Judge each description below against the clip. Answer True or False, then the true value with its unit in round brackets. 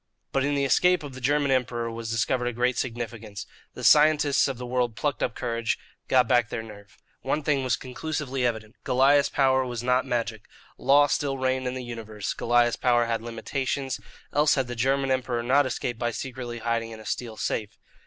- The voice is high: False (125 Hz)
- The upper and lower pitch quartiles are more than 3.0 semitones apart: False (2.6 semitones)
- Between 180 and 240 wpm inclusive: True (195 wpm)